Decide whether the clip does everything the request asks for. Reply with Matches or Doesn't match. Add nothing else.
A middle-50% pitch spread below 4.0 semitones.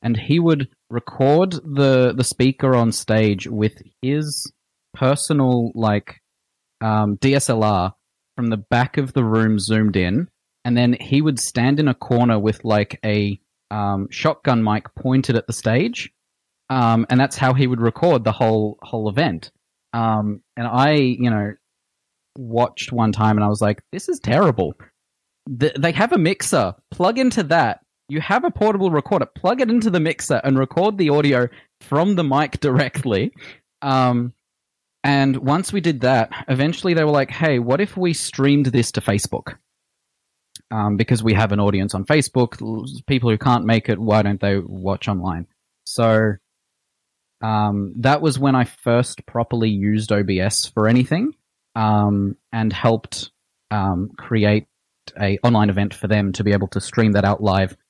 Doesn't match